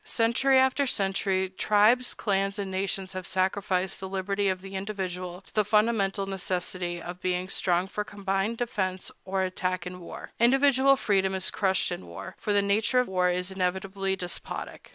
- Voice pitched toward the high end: Yes, high, 195 Hz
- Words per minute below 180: Yes, average, 170 wpm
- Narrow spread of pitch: Yes, narrow, 2.0 semitones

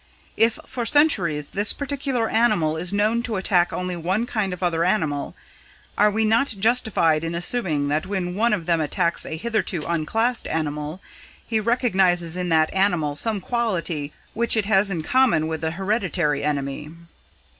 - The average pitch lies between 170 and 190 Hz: Yes, medium, 185 Hz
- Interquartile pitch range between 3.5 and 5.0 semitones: No, wide, 5.6 semitones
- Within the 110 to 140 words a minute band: No, average, 165 wpm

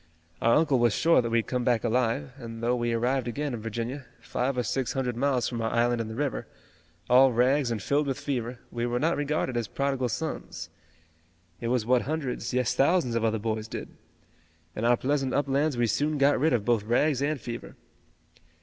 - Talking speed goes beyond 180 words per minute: Yes, fast, 205 wpm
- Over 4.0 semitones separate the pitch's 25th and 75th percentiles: No, average, 3.0 semitones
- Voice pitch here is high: No, low, 125 Hz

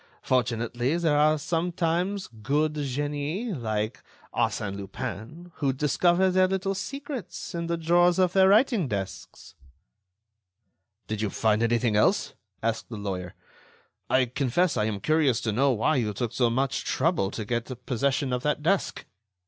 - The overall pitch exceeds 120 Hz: Yes, medium, 140 Hz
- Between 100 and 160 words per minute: Yes, average, 150 wpm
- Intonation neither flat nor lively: No, wide, 7.0 semitones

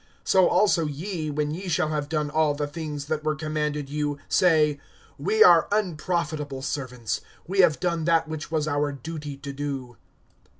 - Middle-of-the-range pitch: Yes, medium, 150 Hz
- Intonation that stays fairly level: Yes, narrow, 2.1 semitones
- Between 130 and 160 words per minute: No, average, 170 wpm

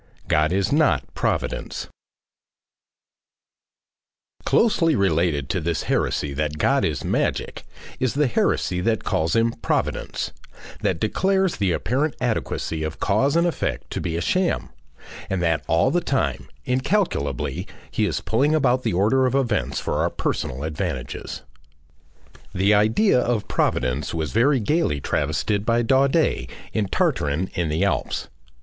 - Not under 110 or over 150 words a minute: Yes, average, 140 wpm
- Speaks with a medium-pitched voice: No, low, 105 Hz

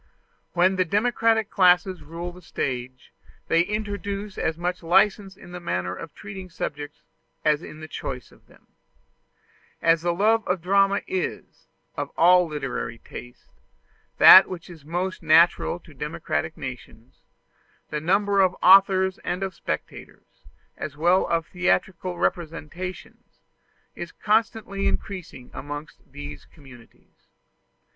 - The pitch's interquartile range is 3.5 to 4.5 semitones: Yes, average, 3.9 semitones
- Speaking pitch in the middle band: Yes, medium, 175 Hz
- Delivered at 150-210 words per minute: No, slow, 135 wpm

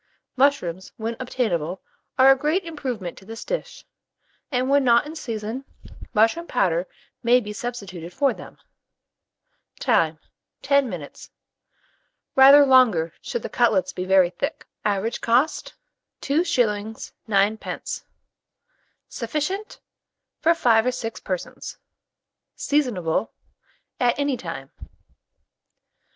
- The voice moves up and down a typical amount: No, wide, 5.9 semitones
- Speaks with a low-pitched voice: No, high, 240 Hz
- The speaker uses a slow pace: Yes, slow, 110 wpm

